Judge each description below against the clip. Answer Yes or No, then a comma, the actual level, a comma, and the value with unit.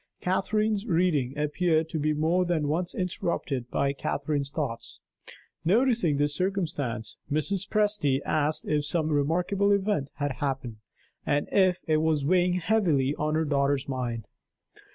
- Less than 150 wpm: Yes, slow, 135 wpm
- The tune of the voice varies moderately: Yes, average, 4.3 semitones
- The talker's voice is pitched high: No, medium, 155 Hz